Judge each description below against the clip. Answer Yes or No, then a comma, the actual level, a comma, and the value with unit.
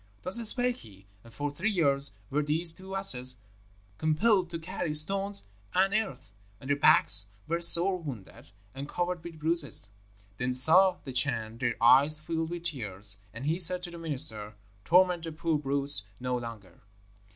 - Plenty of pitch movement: Yes, wide, 5.7 semitones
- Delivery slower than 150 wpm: No, average, 165 wpm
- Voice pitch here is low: No, medium, 155 Hz